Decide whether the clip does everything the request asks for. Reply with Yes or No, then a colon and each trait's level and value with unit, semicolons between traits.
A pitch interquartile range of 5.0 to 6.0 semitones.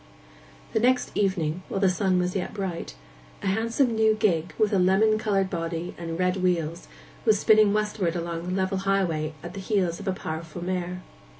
No: average, 3.2 semitones